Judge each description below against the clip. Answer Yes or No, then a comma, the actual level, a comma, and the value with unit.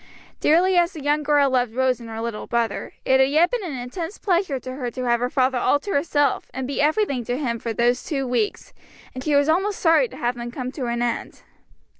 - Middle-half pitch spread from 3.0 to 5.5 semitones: Yes, average, 4.2 semitones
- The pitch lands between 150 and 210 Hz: No, very high, 265 Hz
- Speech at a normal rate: No, fast, 240 wpm